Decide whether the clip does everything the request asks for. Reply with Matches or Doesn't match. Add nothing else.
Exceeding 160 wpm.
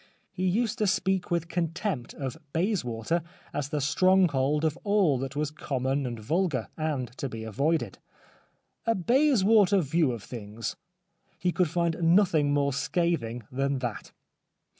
Doesn't match